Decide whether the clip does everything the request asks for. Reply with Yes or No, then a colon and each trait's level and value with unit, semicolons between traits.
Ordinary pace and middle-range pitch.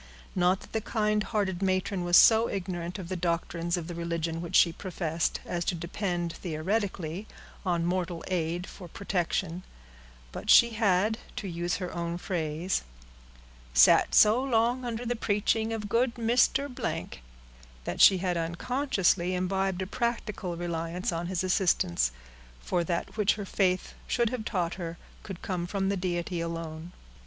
Yes: average, 155 wpm; medium, 180 Hz